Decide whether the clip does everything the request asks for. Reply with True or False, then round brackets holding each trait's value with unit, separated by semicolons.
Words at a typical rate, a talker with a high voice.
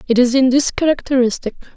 True (170 wpm; 255 Hz)